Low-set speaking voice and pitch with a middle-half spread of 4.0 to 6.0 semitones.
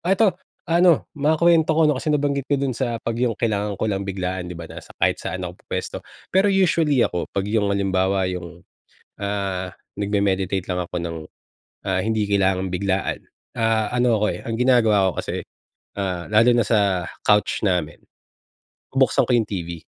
Yes: low, 105 Hz; average, 4.9 semitones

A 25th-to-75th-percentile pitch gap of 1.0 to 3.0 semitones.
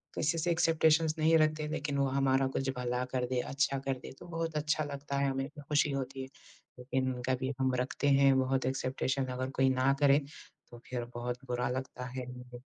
Yes: narrow, 2.4 semitones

